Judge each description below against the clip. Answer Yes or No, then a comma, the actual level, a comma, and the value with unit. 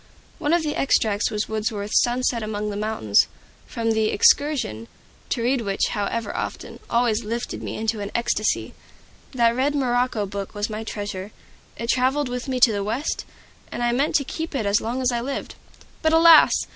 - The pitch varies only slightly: No, average, 3.4 semitones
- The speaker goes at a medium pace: Yes, average, 185 wpm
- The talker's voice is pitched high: Yes, high, 230 Hz